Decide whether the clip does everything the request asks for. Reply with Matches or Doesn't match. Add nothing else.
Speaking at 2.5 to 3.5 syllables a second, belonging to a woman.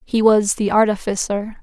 Doesn't match